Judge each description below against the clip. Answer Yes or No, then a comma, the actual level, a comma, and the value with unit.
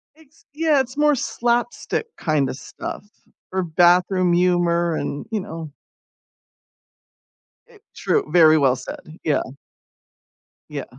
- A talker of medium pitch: Yes, medium, 175 Hz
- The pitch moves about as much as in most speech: No, wide, 7.2 semitones